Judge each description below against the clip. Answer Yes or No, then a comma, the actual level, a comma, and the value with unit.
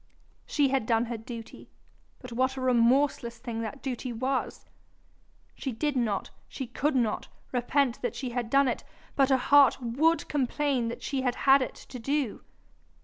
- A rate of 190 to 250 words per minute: No, average, 170 wpm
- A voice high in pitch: Yes, very high, 255 Hz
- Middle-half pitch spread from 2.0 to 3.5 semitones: Yes, narrow, 2.6 semitones